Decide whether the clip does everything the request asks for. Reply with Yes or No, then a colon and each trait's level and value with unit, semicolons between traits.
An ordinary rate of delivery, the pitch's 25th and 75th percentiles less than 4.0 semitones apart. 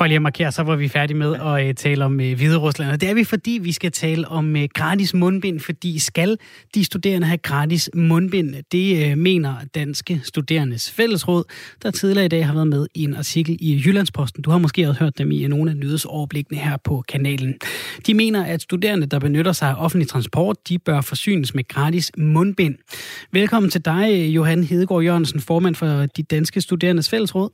Yes: average, 190 wpm; average, 3.4 semitones